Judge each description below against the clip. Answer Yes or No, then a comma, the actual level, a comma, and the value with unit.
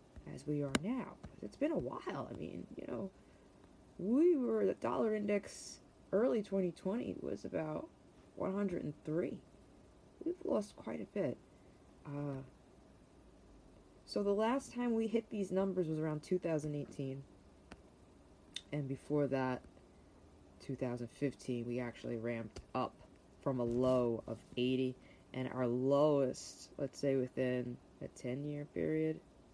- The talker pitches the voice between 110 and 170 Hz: Yes, low, 135 Hz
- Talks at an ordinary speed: No, slow, 125 wpm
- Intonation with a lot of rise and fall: Yes, wide, 7.7 semitones